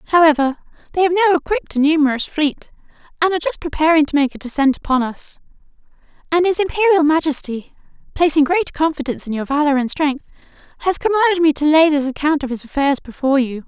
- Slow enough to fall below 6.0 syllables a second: No, 6.4 syllables/s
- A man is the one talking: No, female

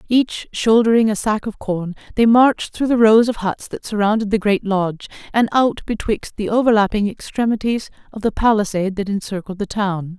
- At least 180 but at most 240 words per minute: Yes, average, 185 wpm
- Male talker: No, female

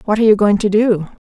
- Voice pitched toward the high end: Yes, high, 210 Hz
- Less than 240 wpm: No, fast, 280 wpm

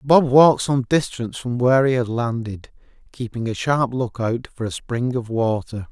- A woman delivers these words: No, male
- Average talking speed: Yes, average, 185 wpm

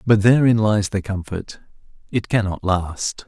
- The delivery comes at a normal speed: No, slow, 130 wpm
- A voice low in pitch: Yes, low, 100 Hz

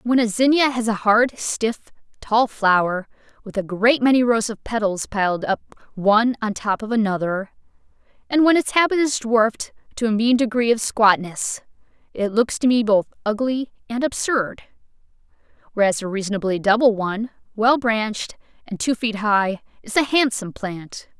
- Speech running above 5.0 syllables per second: No, 4.9 syllables/s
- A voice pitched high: Yes, high, 225 Hz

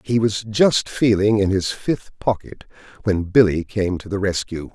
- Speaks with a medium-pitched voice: No, low, 100 Hz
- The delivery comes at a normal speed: Yes, average, 175 wpm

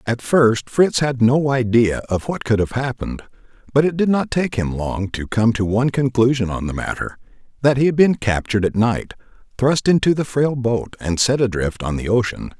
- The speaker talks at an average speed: No, fast, 210 wpm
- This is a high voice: No, low, 120 Hz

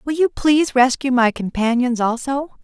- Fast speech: No, average, 160 wpm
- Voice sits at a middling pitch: No, very high, 260 Hz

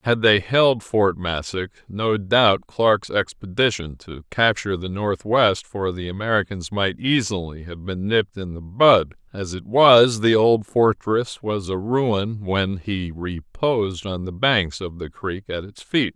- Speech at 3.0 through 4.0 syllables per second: Yes, 3.9 syllables/s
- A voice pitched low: Yes, low, 100 Hz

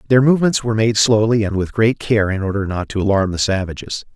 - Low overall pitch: Yes, low, 105 Hz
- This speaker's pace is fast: Yes, fast, 230 wpm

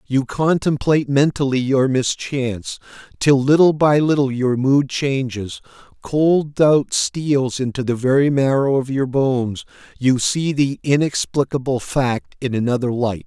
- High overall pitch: No, low, 135 Hz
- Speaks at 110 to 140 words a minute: Yes, slow, 135 wpm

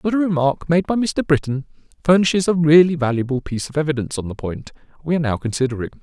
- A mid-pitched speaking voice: Yes, medium, 150 Hz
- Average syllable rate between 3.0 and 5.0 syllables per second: No, 7.0 syllables/s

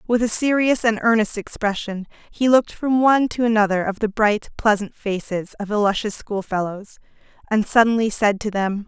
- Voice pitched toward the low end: No, high, 215 Hz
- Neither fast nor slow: Yes, average, 170 wpm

